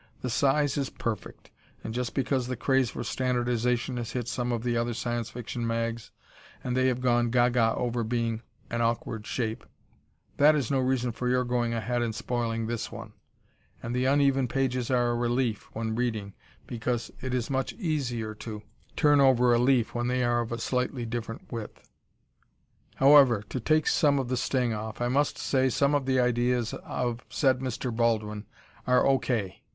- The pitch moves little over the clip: Yes, narrow, 1.8 semitones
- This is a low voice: Yes, low, 120 Hz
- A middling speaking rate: Yes, average, 185 wpm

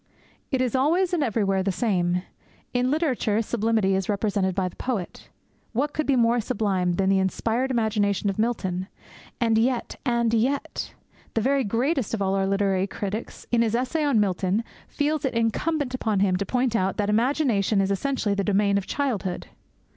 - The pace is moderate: Yes, average, 175 wpm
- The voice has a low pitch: No, high, 220 Hz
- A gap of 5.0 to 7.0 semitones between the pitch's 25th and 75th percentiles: No, average, 4.5 semitones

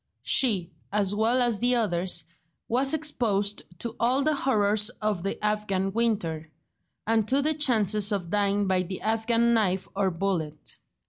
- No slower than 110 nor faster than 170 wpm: Yes, average, 150 wpm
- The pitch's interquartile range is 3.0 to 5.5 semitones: Yes, average, 3.5 semitones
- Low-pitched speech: No, high, 210 Hz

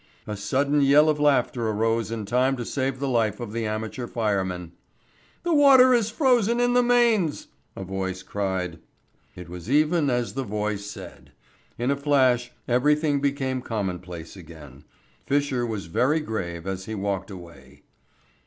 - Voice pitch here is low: Yes, low, 120 Hz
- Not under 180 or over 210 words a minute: No, average, 155 wpm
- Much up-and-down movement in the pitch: Yes, wide, 6.7 semitones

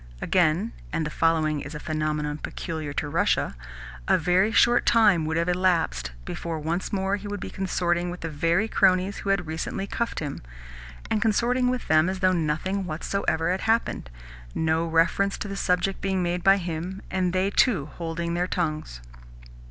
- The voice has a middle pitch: Yes, medium, 175 Hz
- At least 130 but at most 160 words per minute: No, average, 175 wpm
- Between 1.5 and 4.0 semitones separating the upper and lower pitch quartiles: Yes, average, 3.4 semitones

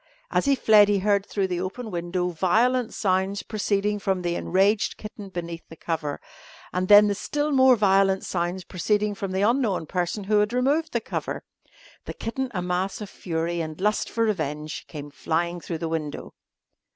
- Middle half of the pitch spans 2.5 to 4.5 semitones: Yes, average, 3.4 semitones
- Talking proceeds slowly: No, average, 175 wpm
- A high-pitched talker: Yes, high, 195 Hz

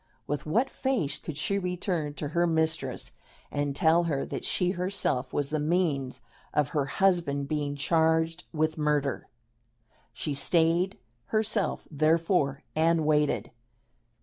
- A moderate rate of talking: No, slow, 130 wpm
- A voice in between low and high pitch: Yes, medium, 160 Hz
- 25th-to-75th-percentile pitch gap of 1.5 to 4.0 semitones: Yes, average, 3.1 semitones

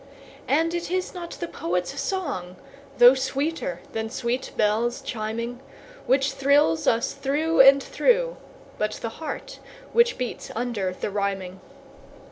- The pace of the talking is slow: Yes, slow, 130 wpm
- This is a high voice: Yes, very high, 250 Hz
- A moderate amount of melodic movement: No, wide, 6.4 semitones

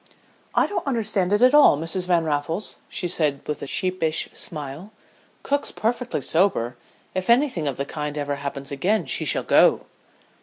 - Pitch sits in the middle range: Yes, medium, 165 Hz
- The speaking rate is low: No, average, 165 wpm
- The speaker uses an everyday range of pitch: No, wide, 6.5 semitones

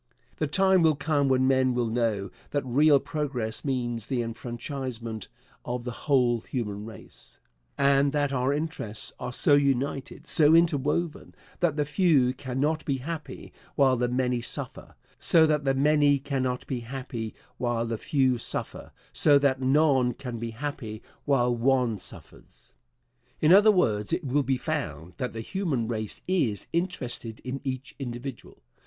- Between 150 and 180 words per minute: Yes, average, 155 wpm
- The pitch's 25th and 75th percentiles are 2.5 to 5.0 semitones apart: Yes, average, 3.4 semitones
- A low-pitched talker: Yes, low, 130 Hz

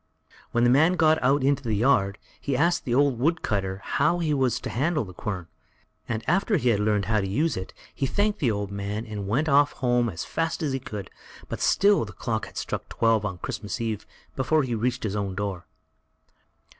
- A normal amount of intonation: No, wide, 5.9 semitones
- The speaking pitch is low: Yes, low, 120 Hz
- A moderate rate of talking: No, fast, 210 wpm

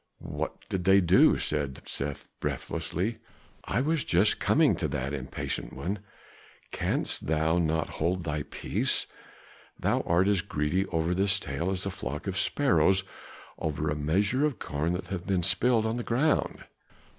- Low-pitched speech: Yes, very low, 90 Hz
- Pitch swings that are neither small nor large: Yes, average, 4.2 semitones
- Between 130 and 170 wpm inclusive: Yes, average, 155 wpm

